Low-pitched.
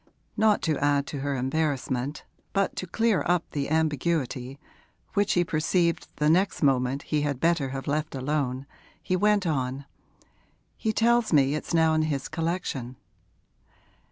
No: medium, 150 Hz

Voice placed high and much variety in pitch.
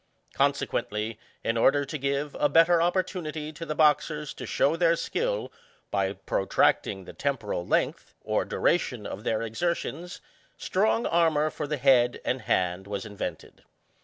No: medium, 145 Hz; wide, 6.7 semitones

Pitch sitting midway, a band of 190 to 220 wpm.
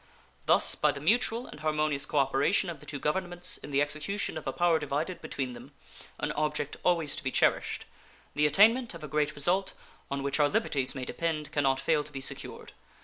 Yes: medium, 150 Hz; fast, 205 wpm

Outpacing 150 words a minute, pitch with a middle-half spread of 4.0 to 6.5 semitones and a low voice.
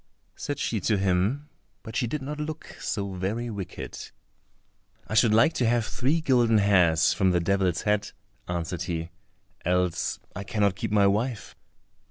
Yes: average, 160 wpm; average, 4.6 semitones; low, 105 Hz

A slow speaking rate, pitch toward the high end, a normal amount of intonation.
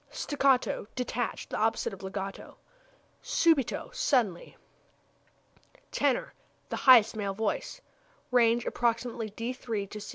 Yes: slow, 100 wpm; high, 230 Hz; average, 3.4 semitones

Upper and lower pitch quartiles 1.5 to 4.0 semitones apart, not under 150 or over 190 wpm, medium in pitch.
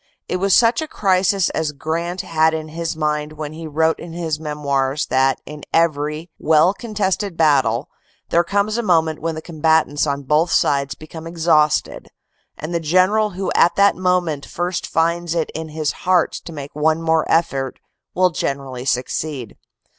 Yes: narrow, 2.6 semitones; average, 170 wpm; medium, 160 Hz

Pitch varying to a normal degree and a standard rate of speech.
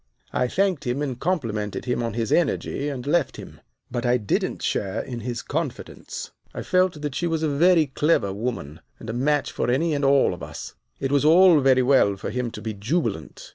No: average, 4.6 semitones; fast, 210 wpm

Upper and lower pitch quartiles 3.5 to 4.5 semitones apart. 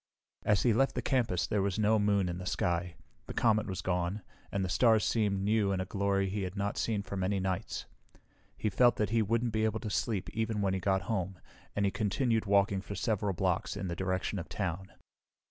No: narrow, 2.4 semitones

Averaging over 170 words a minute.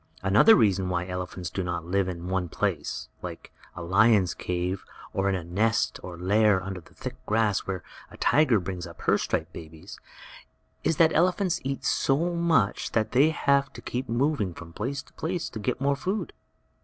Yes: average, 185 wpm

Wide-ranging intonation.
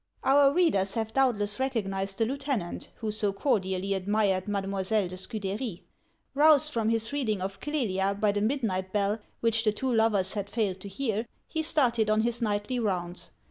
No: average, 3.8 semitones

